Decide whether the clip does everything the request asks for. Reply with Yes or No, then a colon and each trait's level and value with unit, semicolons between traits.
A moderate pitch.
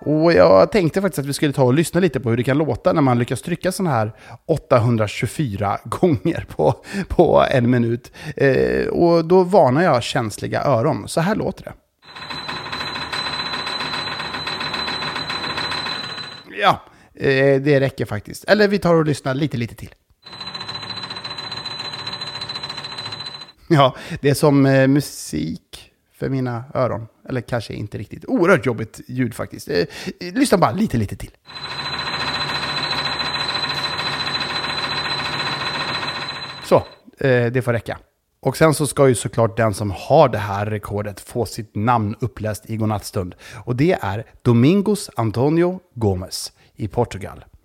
No: low, 130 Hz